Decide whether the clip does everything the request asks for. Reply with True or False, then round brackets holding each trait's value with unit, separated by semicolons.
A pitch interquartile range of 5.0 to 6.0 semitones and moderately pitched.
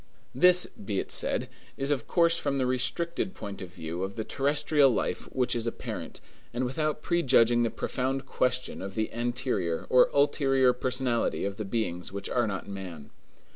False (5.3 semitones; 125 Hz)